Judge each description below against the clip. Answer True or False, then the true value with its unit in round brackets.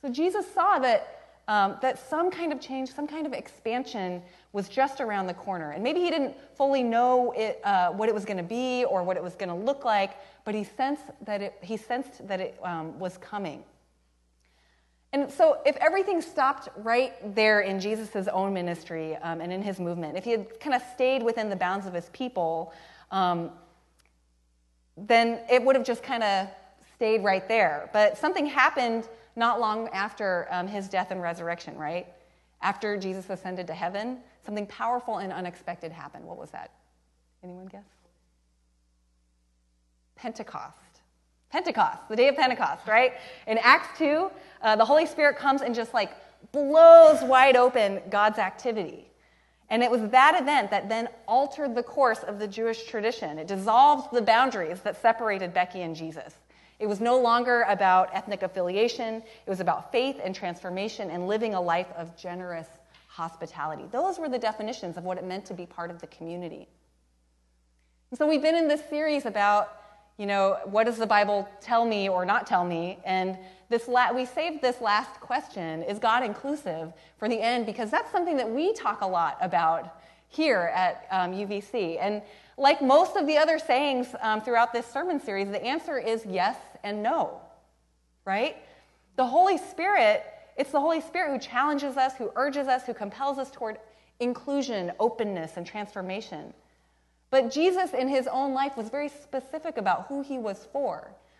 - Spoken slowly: False (180 wpm)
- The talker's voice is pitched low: False (215 Hz)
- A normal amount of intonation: False (6.2 semitones)